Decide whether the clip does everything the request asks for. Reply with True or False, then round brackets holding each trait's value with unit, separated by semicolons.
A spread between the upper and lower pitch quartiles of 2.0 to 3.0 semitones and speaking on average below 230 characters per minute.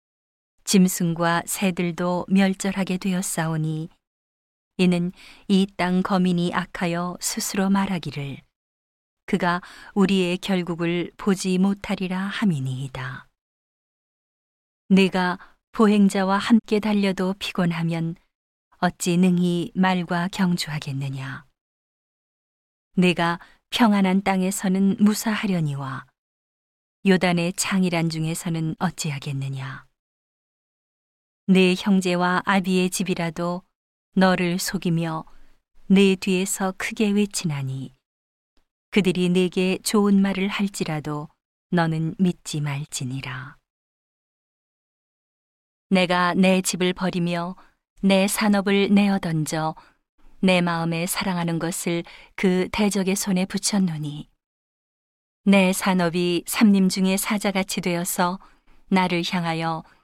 True (2.6 semitones; 210 characters per minute)